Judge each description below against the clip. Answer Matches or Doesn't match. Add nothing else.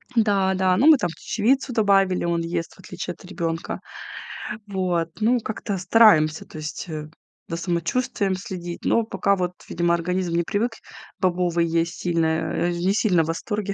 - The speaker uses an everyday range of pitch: Matches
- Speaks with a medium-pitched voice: Matches